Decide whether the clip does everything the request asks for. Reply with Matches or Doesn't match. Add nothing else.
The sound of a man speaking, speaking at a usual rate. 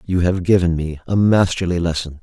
Matches